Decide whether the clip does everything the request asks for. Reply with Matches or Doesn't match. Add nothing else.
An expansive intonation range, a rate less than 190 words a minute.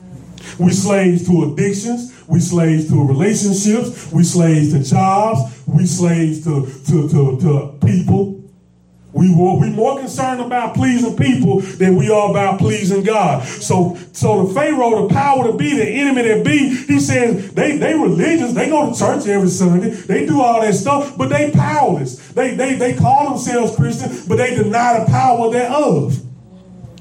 Matches